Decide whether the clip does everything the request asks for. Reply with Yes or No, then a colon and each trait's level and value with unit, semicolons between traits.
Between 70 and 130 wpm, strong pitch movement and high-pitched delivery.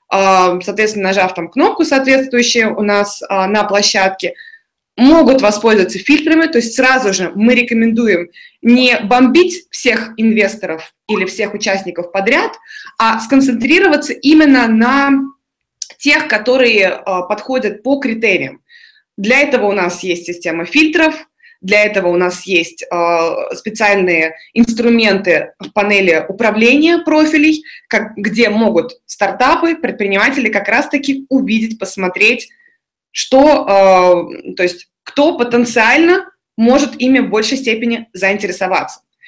Yes: slow, 110 wpm; wide, 6.0 semitones; high, 230 Hz